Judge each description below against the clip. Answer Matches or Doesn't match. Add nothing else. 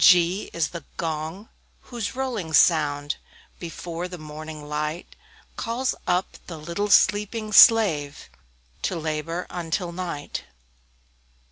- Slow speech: Matches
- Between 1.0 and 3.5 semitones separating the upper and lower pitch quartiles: Doesn't match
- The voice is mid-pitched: Matches